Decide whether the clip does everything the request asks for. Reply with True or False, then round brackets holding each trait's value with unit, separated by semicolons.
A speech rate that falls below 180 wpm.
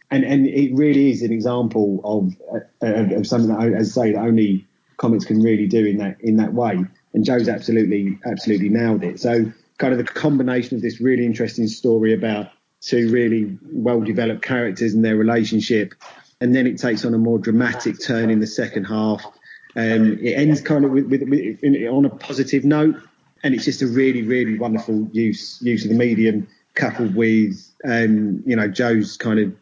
False (200 wpm)